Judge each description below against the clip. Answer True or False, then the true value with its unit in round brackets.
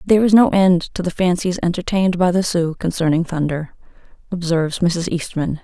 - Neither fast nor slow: True (170 wpm)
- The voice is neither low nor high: True (175 Hz)